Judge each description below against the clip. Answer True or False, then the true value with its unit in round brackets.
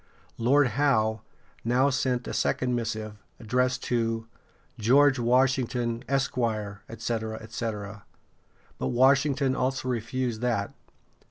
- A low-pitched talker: True (120 Hz)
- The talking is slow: True (100 wpm)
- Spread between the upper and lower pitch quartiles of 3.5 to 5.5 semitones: False (2.7 semitones)